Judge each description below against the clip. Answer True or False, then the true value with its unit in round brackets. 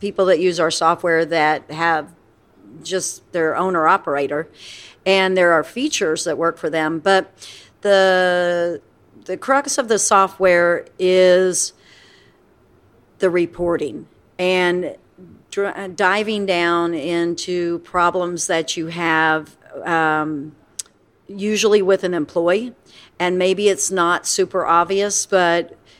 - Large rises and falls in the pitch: False (2.4 semitones)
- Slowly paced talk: True (115 wpm)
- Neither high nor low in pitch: True (175 Hz)